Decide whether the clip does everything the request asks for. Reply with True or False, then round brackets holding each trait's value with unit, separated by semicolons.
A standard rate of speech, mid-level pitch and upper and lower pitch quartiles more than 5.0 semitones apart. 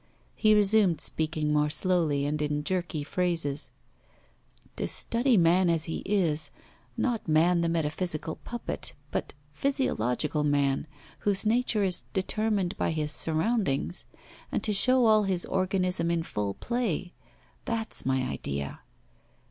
False (130 wpm; 175 Hz; 5.5 semitones)